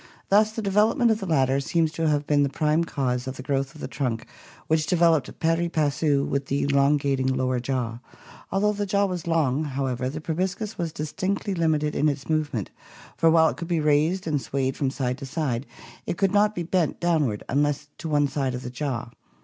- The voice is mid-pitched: Yes, medium, 150 Hz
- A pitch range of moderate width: Yes, average, 3.8 semitones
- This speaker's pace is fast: Yes, fast, 210 wpm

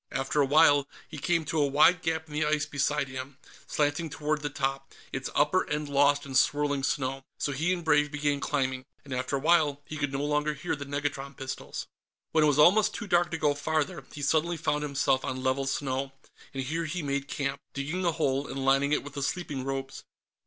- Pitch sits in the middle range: Yes, medium, 145 Hz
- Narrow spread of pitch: Yes, narrow, 2.0 semitones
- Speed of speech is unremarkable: No, fast, 215 wpm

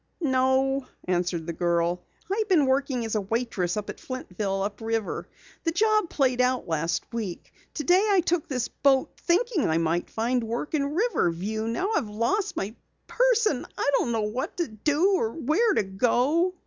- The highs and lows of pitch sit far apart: Yes, wide, 7.9 semitones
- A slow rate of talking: No, average, 175 wpm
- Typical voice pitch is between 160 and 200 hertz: No, very high, 250 Hz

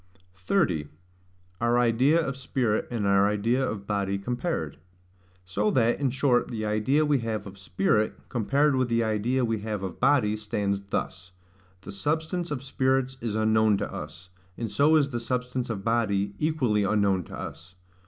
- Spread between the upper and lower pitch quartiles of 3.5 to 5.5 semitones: Yes, average, 4.5 semitones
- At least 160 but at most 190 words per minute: Yes, average, 165 wpm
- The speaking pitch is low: Yes, low, 115 Hz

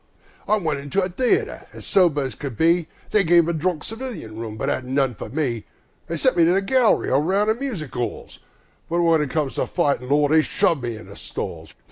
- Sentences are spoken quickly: Yes, fast, 225 wpm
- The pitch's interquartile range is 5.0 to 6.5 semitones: Yes, average, 5.3 semitones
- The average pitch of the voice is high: No, medium, 160 Hz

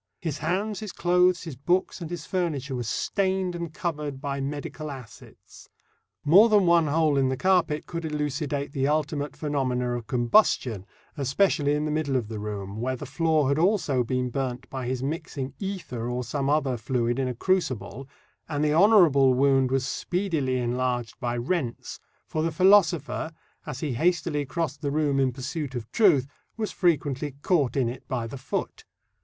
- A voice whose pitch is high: No, medium, 145 Hz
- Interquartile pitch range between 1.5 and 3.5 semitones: No, average, 4.5 semitones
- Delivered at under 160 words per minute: No, average, 175 wpm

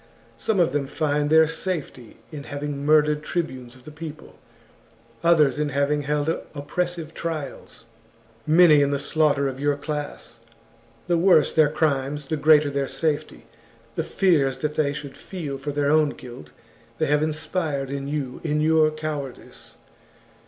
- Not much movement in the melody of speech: Yes, narrow, 1.8 semitones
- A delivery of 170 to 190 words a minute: No, average, 155 wpm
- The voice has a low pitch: No, medium, 150 Hz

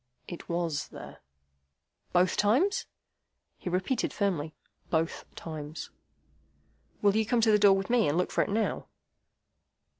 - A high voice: Yes, high, 195 Hz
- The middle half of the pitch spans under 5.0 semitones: Yes, average, 4.6 semitones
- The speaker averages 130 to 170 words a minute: Yes, average, 140 wpm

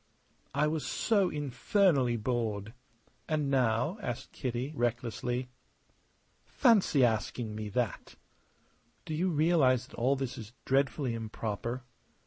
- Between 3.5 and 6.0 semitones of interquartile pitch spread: Yes, average, 4.4 semitones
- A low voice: Yes, low, 125 Hz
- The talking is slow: Yes, slow, 110 wpm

